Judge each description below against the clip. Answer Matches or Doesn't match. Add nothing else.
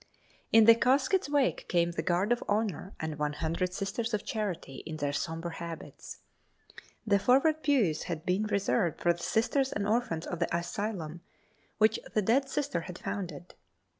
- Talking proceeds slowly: Doesn't match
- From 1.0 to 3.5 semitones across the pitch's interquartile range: Doesn't match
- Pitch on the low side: Doesn't match